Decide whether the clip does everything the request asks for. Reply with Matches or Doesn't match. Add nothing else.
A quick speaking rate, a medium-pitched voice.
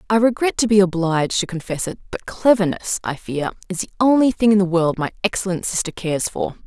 Doesn't match